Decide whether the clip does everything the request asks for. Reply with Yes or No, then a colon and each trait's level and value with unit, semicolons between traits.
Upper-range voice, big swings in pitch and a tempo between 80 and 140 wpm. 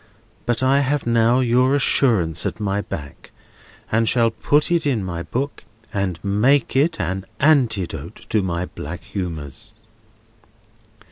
No: low, 110 Hz; wide, 6.3 semitones; slow, 135 wpm